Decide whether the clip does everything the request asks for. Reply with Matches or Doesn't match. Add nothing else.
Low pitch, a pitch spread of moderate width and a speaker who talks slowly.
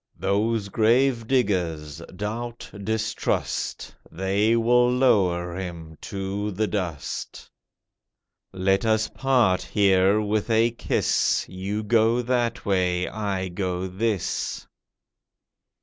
Matches